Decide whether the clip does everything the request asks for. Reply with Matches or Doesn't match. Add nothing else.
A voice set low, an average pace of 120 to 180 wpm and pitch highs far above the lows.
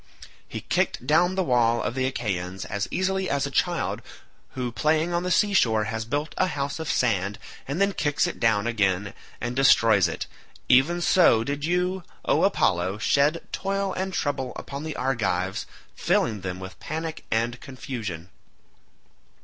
Matches